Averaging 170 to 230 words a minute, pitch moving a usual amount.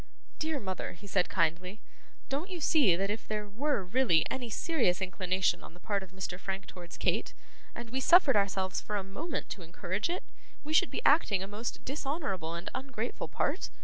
No: average, 190 wpm; wide, 6.4 semitones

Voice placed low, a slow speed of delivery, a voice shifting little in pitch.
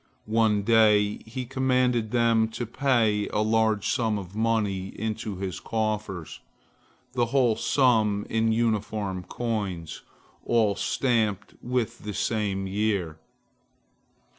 Yes: low, 110 Hz; slow, 115 wpm; narrow, 2.2 semitones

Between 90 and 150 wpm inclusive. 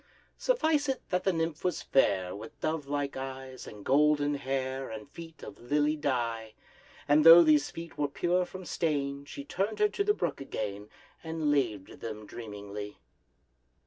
No: average, 165 wpm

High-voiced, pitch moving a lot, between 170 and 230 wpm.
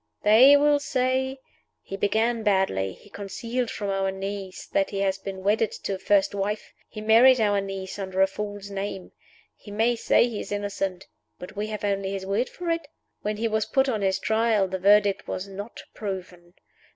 No: high, 205 Hz; narrow, 2.4 semitones; average, 190 wpm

